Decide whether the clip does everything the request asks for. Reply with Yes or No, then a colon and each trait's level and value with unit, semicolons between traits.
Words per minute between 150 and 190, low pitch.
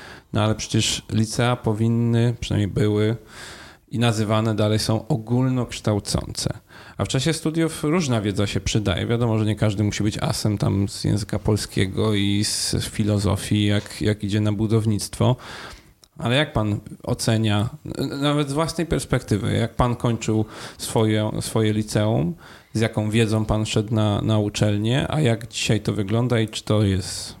Yes: average, 155 wpm; low, 110 Hz